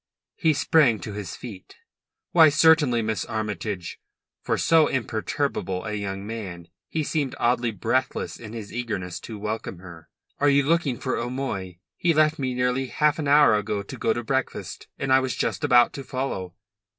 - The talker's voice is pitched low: Yes, low, 120 Hz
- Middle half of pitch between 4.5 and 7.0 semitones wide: Yes, average, 5.3 semitones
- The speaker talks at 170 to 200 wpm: Yes, average, 175 wpm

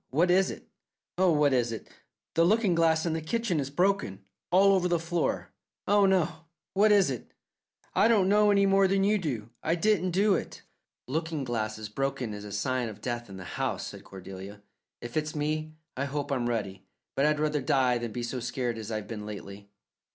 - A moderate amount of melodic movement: No, wide, 7.7 semitones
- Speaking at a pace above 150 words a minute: Yes, fast, 205 wpm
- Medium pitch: Yes, medium, 150 Hz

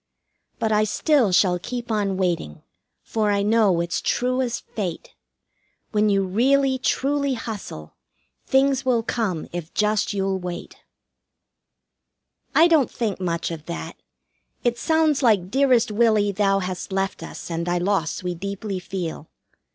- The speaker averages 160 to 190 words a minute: No, average, 145 wpm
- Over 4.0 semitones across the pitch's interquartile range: Yes, average, 4.9 semitones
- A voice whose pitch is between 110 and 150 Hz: No, high, 205 Hz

